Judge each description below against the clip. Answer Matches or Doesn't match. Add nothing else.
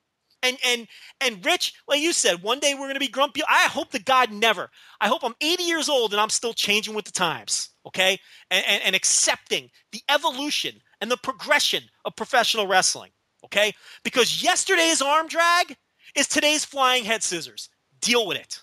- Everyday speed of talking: Matches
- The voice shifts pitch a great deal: Matches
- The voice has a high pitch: Matches